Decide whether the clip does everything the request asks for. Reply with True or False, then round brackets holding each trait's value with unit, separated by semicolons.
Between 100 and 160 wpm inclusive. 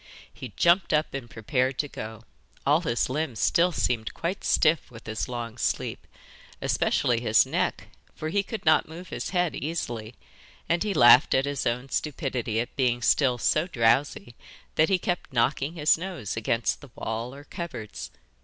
False (170 wpm)